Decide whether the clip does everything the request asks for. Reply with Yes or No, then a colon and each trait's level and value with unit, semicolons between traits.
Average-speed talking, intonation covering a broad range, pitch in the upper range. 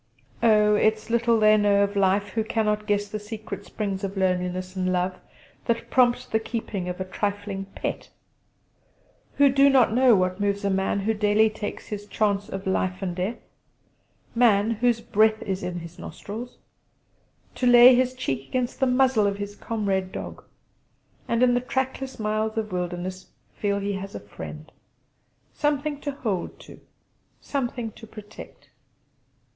No: average, 160 wpm; average, 3.2 semitones; high, 210 Hz